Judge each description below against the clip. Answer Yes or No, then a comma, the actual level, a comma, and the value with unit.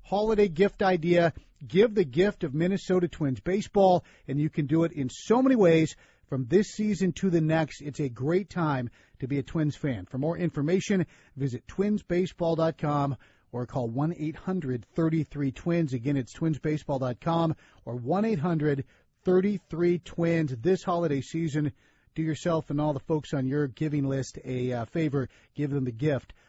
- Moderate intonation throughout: Yes, average, 4.3 semitones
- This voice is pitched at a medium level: Yes, medium, 155 Hz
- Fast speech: No, average, 165 wpm